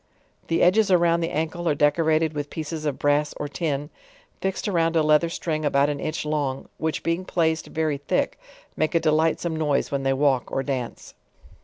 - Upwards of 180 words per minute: Yes, average, 190 wpm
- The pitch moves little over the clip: Yes, narrow, 2.3 semitones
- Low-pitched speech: No, medium, 155 Hz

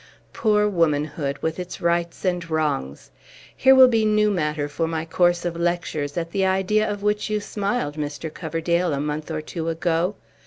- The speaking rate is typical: Yes, average, 180 wpm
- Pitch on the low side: No, medium, 170 Hz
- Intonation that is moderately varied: Yes, average, 4.1 semitones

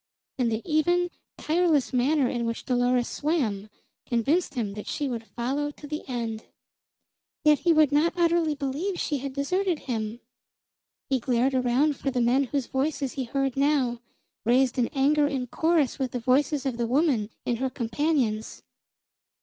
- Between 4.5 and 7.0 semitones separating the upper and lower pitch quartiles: No, average, 3.8 semitones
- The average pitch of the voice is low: No, very high, 270 Hz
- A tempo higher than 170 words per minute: No, average, 165 wpm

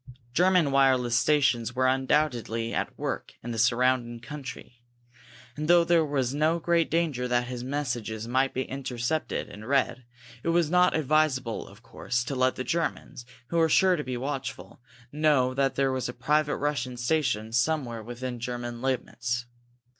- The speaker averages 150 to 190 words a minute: Yes, average, 160 wpm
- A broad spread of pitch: No, average, 3.7 semitones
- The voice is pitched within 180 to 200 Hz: No, low, 130 Hz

